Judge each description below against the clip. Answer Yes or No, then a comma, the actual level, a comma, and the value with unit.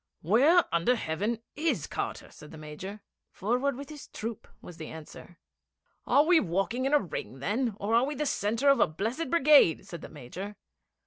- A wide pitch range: Yes, wide, 8.4 semitones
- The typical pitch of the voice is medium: No, high, 220 Hz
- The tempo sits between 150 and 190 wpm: Yes, average, 185 wpm